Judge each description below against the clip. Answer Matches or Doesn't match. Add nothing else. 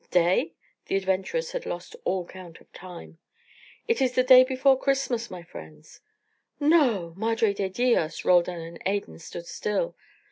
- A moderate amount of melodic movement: Doesn't match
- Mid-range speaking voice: Doesn't match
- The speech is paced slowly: Doesn't match